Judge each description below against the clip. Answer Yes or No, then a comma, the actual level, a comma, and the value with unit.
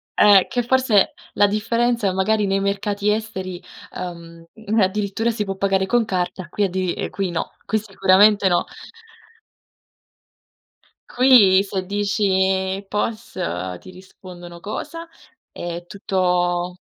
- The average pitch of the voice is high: Yes, high, 195 Hz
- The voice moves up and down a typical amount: No, narrow, 2.2 semitones